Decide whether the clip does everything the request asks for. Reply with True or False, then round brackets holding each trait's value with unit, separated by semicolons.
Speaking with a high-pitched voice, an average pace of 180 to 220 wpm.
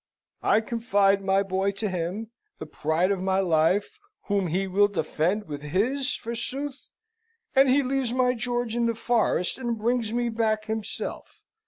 False (215 Hz; 160 wpm)